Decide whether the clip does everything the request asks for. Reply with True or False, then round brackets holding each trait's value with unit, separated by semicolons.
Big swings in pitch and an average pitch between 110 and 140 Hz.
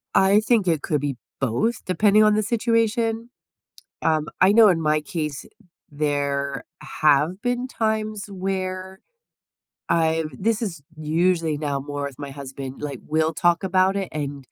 False (6.2 semitones; 170 Hz)